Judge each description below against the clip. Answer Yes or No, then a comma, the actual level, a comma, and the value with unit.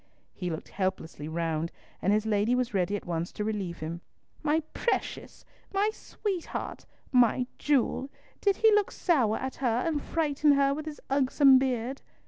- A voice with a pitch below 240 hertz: No, very high, 250 Hz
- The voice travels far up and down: Yes, wide, 7.2 semitones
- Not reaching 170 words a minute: Yes, average, 160 wpm